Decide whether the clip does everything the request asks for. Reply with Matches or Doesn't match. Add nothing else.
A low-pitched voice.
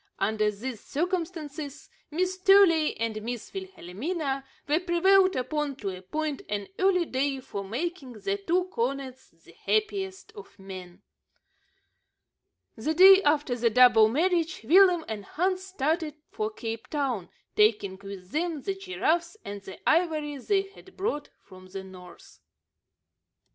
Doesn't match